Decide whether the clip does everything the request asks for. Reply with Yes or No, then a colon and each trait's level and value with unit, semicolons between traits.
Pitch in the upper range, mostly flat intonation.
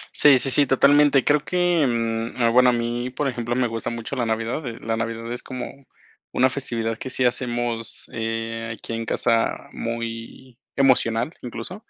No: low, 120 Hz; narrow, 2.3 semitones